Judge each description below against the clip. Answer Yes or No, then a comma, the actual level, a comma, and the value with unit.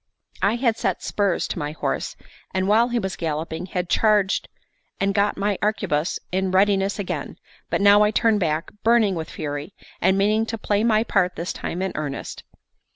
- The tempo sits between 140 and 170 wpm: No, average, 180 wpm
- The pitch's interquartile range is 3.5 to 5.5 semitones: No, average, 3.1 semitones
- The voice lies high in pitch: Yes, high, 195 Hz